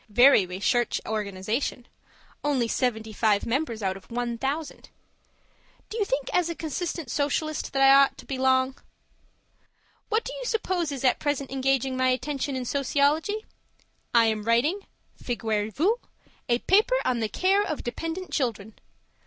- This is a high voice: Yes, very high, 265 Hz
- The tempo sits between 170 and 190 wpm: No, average, 150 wpm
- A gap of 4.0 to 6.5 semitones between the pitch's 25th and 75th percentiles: Yes, average, 5.1 semitones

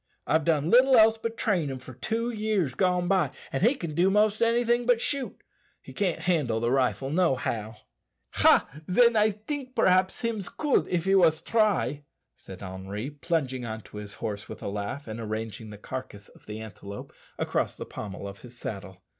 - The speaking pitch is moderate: Yes, medium, 160 Hz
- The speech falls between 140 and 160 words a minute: No, average, 190 wpm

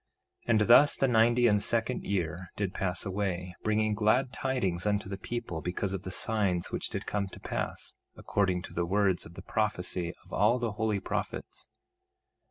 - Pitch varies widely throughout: No, average, 3.4 semitones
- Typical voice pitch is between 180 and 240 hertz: No, low, 100 Hz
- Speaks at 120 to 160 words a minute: No, average, 180 wpm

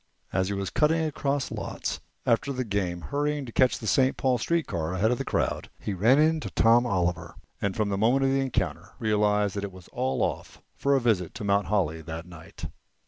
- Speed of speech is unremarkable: No, fast, 215 wpm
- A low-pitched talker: Yes, low, 105 Hz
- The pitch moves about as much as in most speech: No, wide, 6.3 semitones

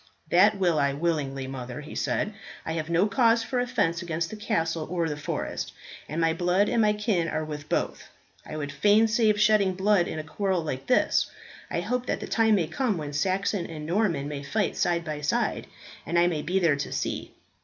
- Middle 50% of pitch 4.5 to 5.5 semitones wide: Yes, average, 5.2 semitones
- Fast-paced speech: Yes, fast, 210 wpm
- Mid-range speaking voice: Yes, medium, 170 Hz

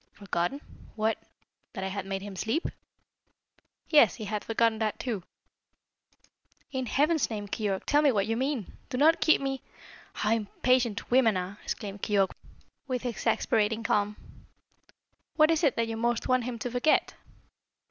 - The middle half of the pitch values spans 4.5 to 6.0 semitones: No, average, 3.9 semitones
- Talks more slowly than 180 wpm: Yes, average, 155 wpm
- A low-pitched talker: No, high, 225 Hz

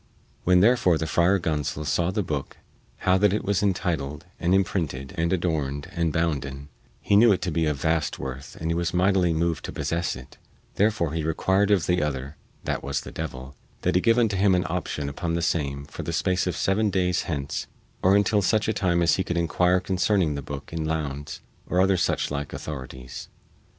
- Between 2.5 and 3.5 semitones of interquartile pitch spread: No, average, 4.2 semitones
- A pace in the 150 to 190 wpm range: No, fast, 205 wpm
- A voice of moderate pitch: No, very low, 85 Hz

